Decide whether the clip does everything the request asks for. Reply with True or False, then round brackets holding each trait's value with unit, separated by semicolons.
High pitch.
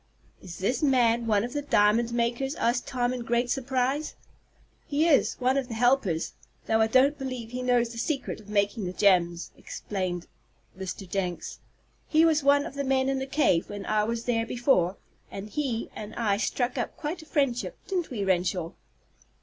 True (240 Hz)